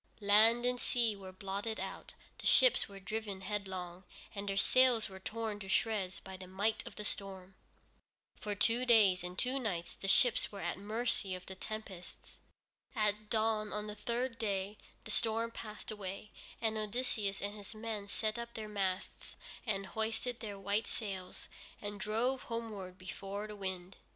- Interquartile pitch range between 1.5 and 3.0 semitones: Yes, narrow, 2.5 semitones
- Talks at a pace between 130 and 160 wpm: No, average, 170 wpm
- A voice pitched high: Yes, high, 210 Hz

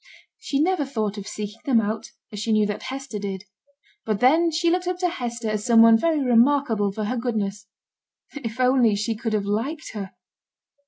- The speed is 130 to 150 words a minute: No, average, 195 wpm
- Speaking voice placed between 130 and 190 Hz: No, high, 230 Hz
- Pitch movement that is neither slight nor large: Yes, average, 4.7 semitones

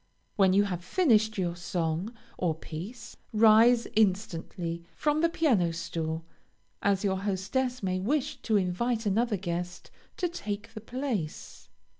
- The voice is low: No, high, 200 Hz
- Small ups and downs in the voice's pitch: No, average, 4.8 semitones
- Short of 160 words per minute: Yes, slow, 135 wpm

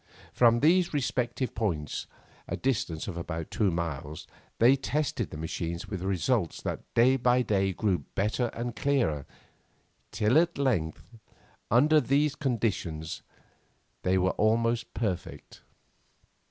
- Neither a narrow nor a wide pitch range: No, wide, 6.5 semitones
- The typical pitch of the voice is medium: No, low, 110 Hz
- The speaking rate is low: Yes, slow, 125 wpm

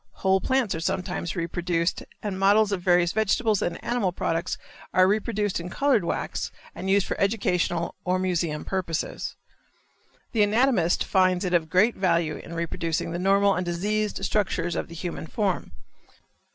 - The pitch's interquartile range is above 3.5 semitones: No, average, 3.1 semitones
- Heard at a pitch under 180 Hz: No, medium, 185 Hz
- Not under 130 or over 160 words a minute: Yes, average, 155 wpm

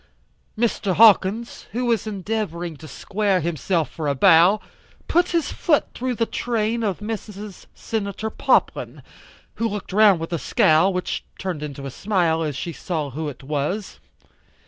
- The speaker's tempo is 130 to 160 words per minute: Yes, average, 155 wpm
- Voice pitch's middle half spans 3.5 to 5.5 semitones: Yes, average, 5.2 semitones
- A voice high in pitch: Yes, high, 195 Hz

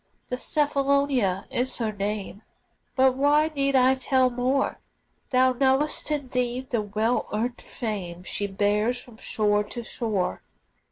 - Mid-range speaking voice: No, high, 245 Hz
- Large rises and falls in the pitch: No, average, 4.0 semitones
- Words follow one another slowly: Yes, slow, 130 wpm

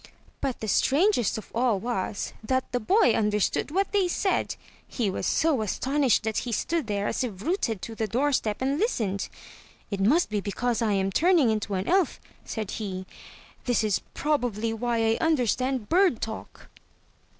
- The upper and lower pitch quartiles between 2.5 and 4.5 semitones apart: No, wide, 5.5 semitones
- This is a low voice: No, high, 235 Hz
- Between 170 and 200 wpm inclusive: Yes, average, 175 wpm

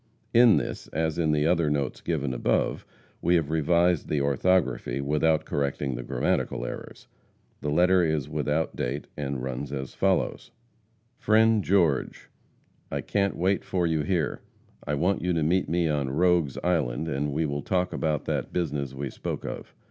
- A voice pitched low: Yes, very low, 80 Hz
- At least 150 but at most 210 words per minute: Yes, average, 165 wpm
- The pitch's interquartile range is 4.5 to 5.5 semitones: No, average, 3.8 semitones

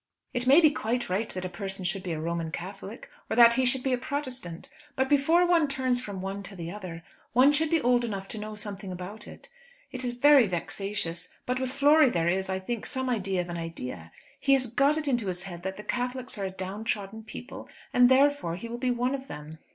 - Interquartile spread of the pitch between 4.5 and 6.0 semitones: Yes, wide, 5.6 semitones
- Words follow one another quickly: Yes, fast, 235 wpm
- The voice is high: Yes, high, 220 Hz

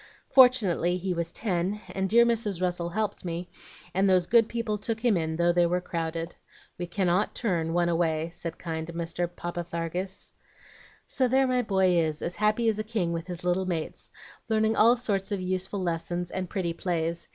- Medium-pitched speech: Yes, medium, 180 Hz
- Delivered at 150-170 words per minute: No, average, 185 wpm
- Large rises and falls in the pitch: No, average, 3.8 semitones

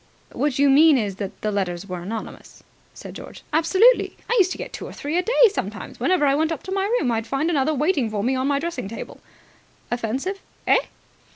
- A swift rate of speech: Yes, fast, 215 wpm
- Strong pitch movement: Yes, wide, 7.4 semitones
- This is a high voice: Yes, very high, 280 Hz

